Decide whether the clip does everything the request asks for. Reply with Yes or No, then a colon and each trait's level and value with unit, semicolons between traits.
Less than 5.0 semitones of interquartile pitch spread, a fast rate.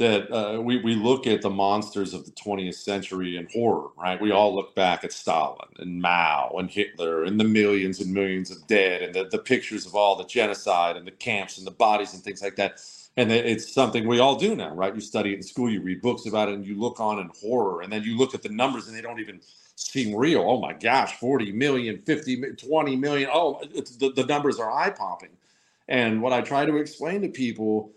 Yes: average, 4.0 semitones; fast, 240 wpm